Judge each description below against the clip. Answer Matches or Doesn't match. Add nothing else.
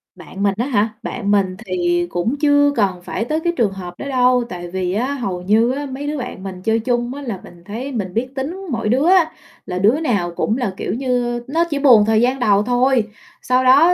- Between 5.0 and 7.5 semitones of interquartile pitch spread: Matches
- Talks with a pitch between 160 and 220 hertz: Doesn't match